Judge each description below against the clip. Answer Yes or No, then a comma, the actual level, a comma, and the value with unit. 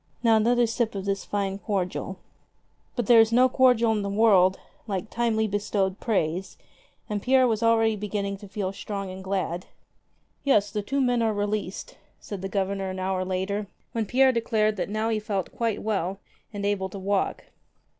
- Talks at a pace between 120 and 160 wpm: No, average, 185 wpm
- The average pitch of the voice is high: Yes, high, 205 Hz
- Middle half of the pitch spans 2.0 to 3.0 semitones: Yes, average, 2.7 semitones